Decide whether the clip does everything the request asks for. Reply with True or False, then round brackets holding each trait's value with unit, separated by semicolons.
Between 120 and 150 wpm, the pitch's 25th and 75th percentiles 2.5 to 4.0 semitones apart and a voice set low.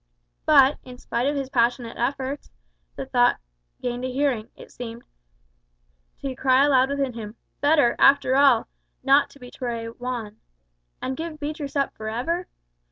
False (145 wpm; 2.8 semitones; 260 Hz)